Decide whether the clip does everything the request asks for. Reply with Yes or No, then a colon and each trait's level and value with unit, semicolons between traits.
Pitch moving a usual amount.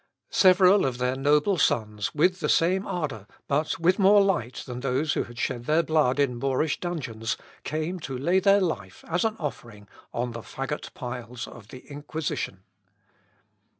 No: wide, 6.1 semitones